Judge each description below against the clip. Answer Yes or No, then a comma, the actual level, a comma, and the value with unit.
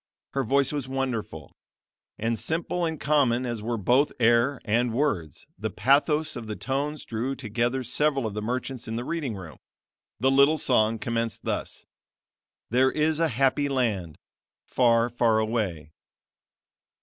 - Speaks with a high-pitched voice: No, low, 125 Hz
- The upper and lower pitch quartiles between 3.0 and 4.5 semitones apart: Yes, average, 3.8 semitones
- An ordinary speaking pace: Yes, average, 150 wpm